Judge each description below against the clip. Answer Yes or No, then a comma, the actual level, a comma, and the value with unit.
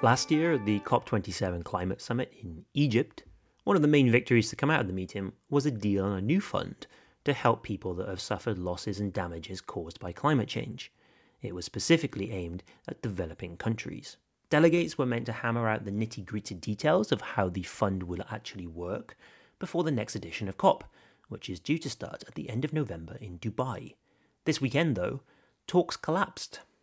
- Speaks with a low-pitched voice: Yes, low, 110 Hz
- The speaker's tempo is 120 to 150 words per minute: No, average, 195 wpm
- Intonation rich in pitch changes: Yes, wide, 6.1 semitones